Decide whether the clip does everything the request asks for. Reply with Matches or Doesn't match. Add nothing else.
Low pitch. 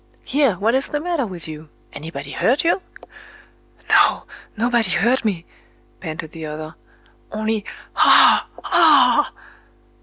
Doesn't match